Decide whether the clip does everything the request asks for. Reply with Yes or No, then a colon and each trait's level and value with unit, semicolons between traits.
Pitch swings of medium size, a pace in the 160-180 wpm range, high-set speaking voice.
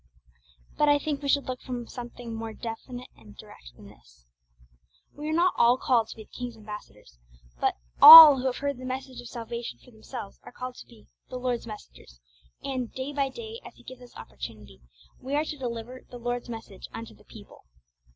No: average, 3.0 semitones; average, 200 wpm; high, 245 Hz